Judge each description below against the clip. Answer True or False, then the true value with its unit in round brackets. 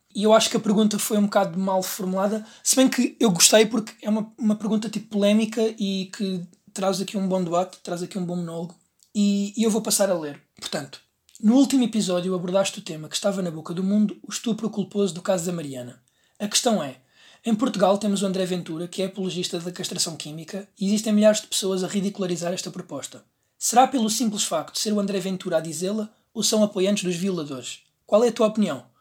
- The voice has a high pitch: True (200 Hz)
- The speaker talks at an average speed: False (220 wpm)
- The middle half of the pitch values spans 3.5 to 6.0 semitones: False (3.0 semitones)